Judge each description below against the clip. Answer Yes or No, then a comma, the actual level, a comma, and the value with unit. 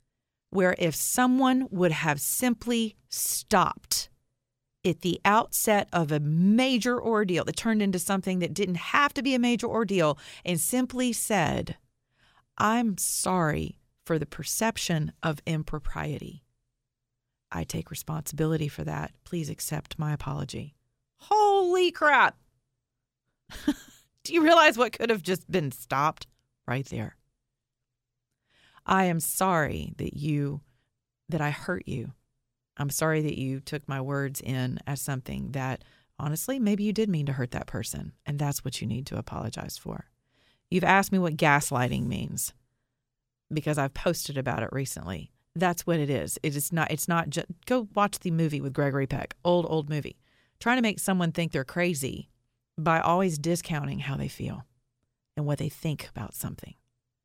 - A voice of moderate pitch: Yes, medium, 150 Hz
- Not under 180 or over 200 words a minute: No, average, 155 wpm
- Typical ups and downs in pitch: No, wide, 6.2 semitones